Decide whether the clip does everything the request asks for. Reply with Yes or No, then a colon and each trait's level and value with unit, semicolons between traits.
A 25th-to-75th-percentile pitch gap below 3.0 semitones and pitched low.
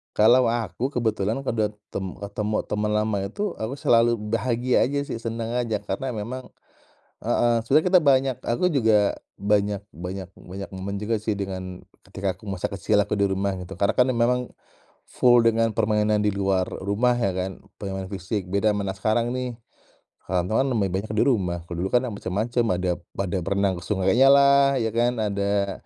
No: average, 3.3 semitones; low, 105 Hz